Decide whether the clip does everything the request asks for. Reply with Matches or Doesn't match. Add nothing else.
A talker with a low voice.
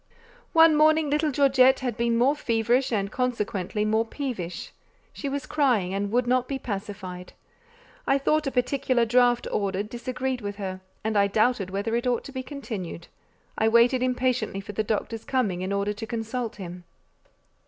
Doesn't match